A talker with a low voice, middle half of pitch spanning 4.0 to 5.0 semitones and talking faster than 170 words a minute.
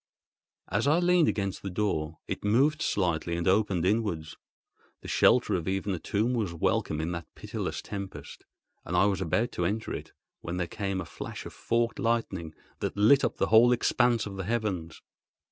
Yes: low, 100 Hz; average, 4.6 semitones; average, 185 wpm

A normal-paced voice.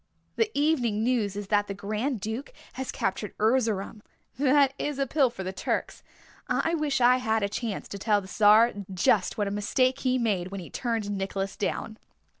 Yes: average, 190 wpm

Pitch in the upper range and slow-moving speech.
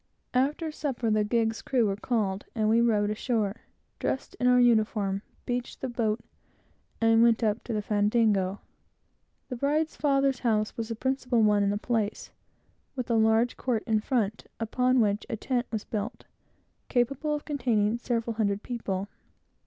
No: high, 225 Hz; average, 160 wpm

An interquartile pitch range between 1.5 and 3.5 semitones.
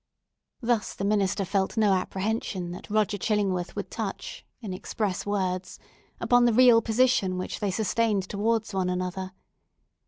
Yes: average, 3.0 semitones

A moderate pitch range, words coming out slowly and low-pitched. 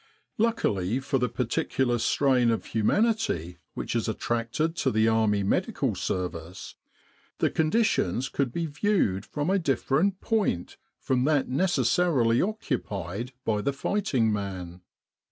No: wide, 7.5 semitones; slow, 125 wpm; low, 125 Hz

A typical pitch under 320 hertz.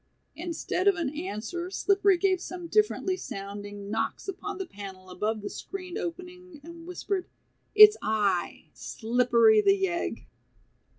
No: very high, 340 Hz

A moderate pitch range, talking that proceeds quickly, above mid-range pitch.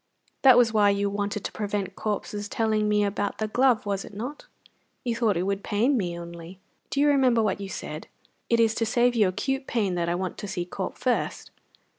Yes: average, 3.3 semitones; fast, 215 wpm; high, 210 Hz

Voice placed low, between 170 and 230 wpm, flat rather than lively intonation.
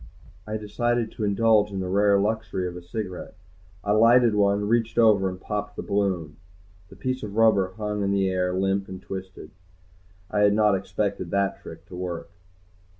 Yes: low, 100 Hz; average, 180 wpm; narrow, 2.3 semitones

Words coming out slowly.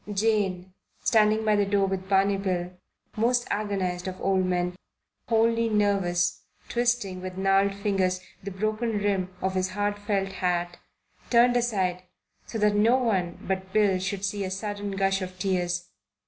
No: average, 155 wpm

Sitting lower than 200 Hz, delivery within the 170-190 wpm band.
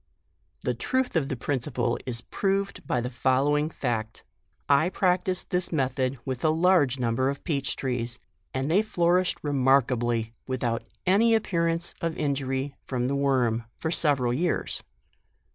No: medium, 140 Hz; average, 145 wpm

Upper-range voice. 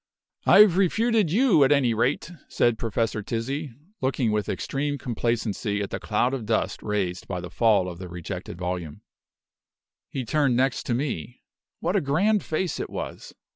No: low, 120 Hz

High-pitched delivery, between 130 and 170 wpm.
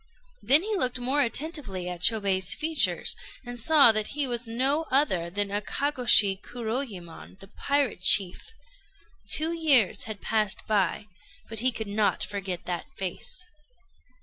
Yes: high, 225 Hz; average, 140 wpm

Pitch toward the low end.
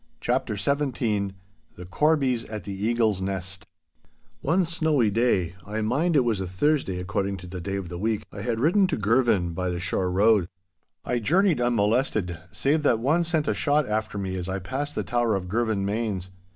Yes: low, 110 Hz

